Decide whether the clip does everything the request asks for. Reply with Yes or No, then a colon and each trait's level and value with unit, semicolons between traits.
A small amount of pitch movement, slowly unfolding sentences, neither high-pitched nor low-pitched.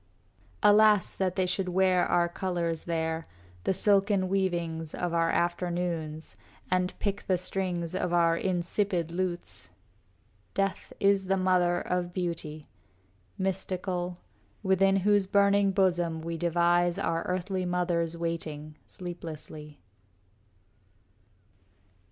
Yes: narrow, 2.1 semitones; slow, 110 wpm; medium, 180 Hz